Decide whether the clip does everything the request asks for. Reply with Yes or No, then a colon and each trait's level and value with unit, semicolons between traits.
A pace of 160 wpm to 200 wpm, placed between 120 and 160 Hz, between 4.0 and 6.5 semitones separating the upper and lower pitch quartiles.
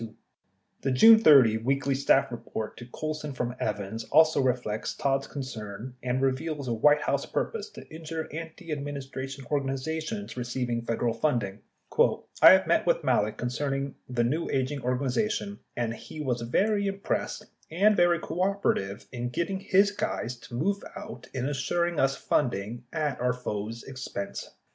No: average, 145 wpm; low, 135 Hz; average, 4.7 semitones